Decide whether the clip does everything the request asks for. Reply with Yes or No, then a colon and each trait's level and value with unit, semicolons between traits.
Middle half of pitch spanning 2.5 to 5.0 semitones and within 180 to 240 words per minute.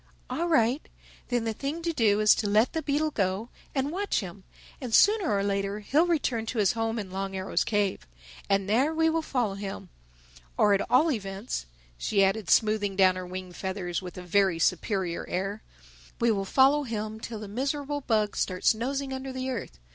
No: wide, 5.4 semitones; average, 185 wpm